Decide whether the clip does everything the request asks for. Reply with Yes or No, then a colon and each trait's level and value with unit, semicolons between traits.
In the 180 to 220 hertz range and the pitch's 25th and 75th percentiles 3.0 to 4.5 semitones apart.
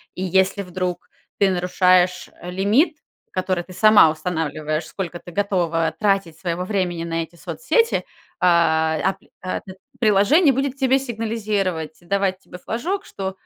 Yes: medium, 185 Hz; average, 3.4 semitones